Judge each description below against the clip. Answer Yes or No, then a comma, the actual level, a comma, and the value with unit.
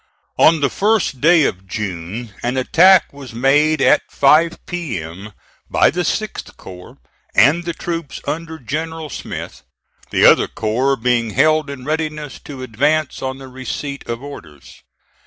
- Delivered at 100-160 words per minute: Yes, average, 145 wpm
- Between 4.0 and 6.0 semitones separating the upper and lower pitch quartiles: Yes, average, 4.8 semitones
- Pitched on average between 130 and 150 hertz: Yes, medium, 140 Hz